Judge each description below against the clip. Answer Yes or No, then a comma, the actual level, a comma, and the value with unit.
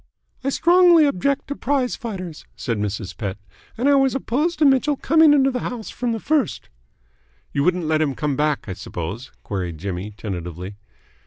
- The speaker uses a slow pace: No, average, 175 wpm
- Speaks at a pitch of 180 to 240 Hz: Yes, medium, 185 Hz